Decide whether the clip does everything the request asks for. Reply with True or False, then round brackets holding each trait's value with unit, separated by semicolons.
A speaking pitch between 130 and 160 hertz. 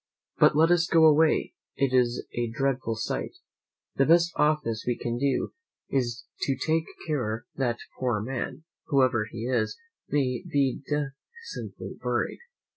True (135 Hz)